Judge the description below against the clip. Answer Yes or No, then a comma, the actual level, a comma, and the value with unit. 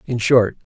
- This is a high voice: No, low, 120 Hz